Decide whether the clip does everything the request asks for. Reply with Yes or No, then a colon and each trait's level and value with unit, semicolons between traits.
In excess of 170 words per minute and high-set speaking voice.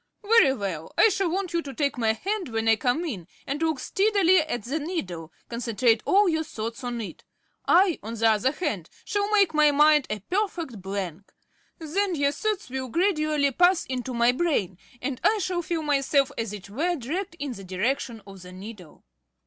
Yes: average, 190 wpm; very high, 280 Hz